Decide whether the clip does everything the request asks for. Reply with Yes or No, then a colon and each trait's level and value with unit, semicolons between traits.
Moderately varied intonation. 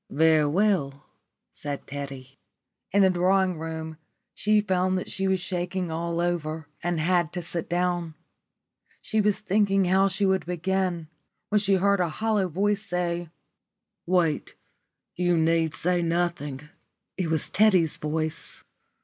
Yes: average, 3.0 semitones